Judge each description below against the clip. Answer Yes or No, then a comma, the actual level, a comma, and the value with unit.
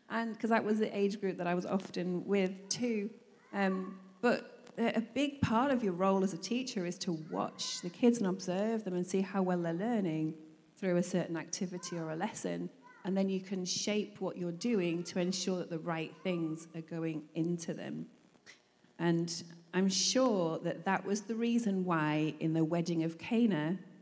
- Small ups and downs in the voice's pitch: No, average, 3.3 semitones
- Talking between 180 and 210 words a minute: Yes, average, 190 wpm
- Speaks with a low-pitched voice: No, medium, 185 Hz